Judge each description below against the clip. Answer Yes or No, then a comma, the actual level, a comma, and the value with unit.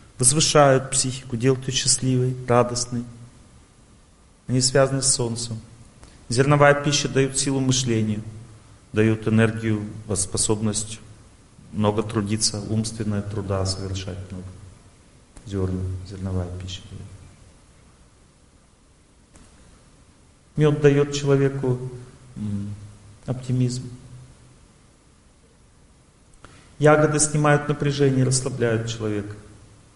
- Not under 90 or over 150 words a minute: No, slow, 75 wpm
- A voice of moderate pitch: No, low, 115 Hz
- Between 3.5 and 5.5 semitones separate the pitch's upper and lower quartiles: Yes, average, 4.0 semitones